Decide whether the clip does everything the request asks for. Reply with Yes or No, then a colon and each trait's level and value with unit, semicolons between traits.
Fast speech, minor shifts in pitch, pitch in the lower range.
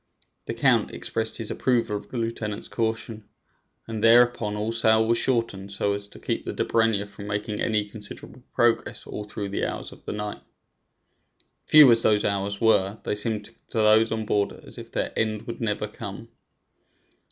No: average, 175 wpm; narrow, 1.8 semitones; low, 110 Hz